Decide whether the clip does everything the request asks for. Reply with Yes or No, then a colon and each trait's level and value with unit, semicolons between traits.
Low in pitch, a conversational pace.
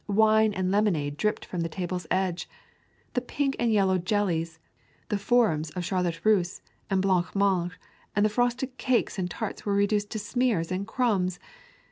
No: high, 195 Hz; average, 165 wpm